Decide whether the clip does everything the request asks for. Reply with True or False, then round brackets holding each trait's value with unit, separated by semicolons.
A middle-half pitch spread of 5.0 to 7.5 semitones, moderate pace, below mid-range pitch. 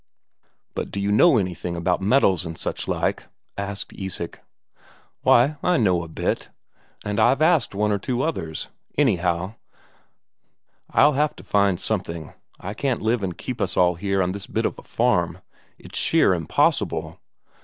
True (5.4 semitones; 160 wpm; 100 Hz)